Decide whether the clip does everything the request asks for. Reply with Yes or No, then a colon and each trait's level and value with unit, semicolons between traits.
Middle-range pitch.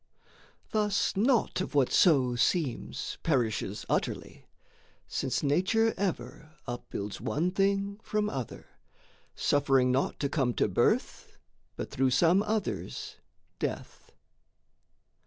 Yes: medium, 155 Hz